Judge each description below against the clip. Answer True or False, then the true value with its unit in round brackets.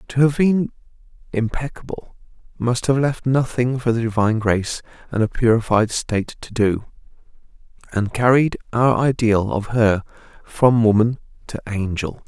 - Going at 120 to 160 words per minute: True (135 wpm)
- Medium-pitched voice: False (115 Hz)